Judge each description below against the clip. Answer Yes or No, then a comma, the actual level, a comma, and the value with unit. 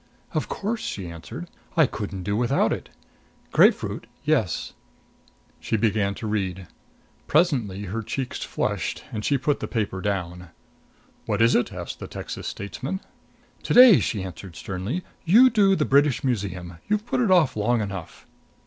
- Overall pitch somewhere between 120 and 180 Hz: No, low, 110 Hz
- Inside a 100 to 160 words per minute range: Yes, average, 155 wpm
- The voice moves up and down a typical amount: No, wide, 7.8 semitones